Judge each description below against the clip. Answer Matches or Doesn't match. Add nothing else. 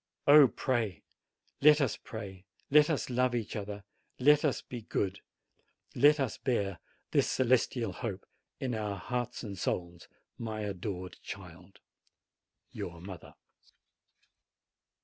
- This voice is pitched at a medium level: Doesn't match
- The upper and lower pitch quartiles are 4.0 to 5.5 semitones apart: Matches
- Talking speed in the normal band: Doesn't match